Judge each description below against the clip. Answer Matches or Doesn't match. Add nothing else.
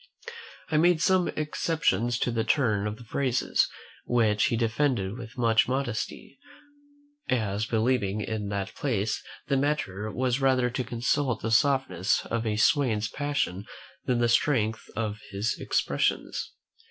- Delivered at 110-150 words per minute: Matches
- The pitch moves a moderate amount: Matches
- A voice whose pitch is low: Matches